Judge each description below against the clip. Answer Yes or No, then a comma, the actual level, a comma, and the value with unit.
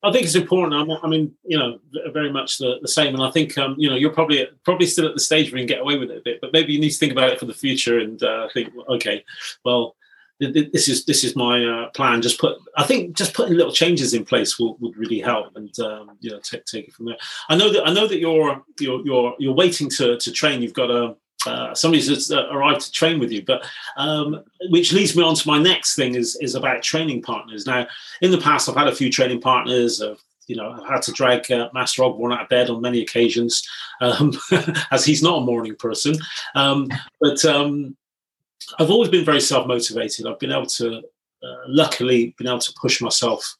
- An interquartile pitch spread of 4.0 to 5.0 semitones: Yes, average, 4.5 semitones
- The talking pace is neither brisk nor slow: No, fast, 240 wpm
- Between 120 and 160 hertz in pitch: Yes, medium, 140 Hz